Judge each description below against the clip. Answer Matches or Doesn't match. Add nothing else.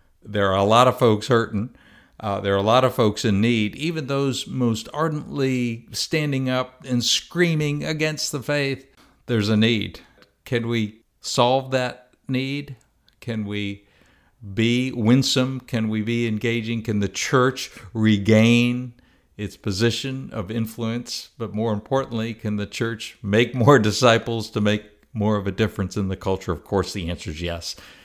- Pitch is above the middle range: Doesn't match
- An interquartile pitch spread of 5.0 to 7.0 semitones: Doesn't match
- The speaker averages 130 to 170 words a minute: Matches